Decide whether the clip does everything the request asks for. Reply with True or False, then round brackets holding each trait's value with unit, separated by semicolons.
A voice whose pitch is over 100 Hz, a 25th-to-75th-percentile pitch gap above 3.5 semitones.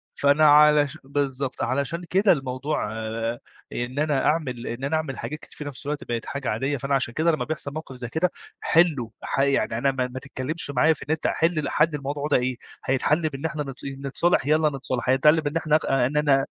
False (140 Hz; 3.0 semitones)